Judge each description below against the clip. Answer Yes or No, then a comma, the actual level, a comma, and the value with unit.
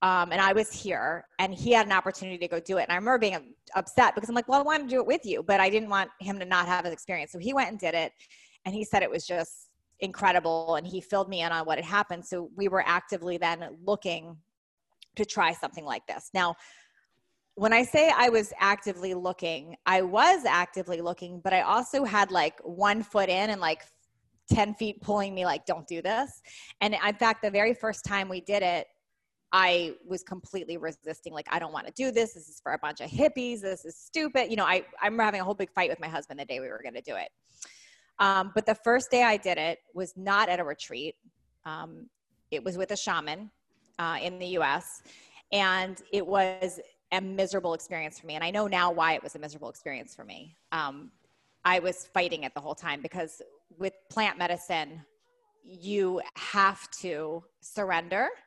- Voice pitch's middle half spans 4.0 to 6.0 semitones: No, average, 3.1 semitones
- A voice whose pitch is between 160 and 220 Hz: Yes, medium, 185 Hz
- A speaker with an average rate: No, fast, 215 wpm